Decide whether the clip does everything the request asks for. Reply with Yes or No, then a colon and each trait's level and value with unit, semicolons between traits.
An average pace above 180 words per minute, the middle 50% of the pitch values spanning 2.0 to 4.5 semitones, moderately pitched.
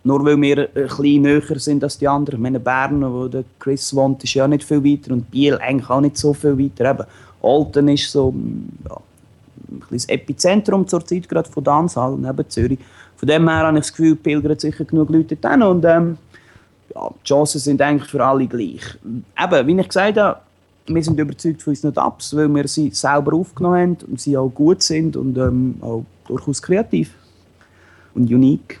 Yes: average, 200 wpm; average, 3.1 semitones; medium, 145 Hz